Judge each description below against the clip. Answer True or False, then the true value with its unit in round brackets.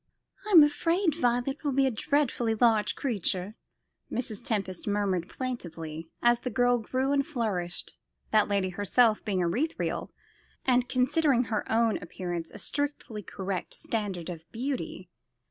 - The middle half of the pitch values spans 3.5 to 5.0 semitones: False (5.4 semitones)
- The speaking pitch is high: True (230 Hz)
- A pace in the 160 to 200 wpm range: False (135 wpm)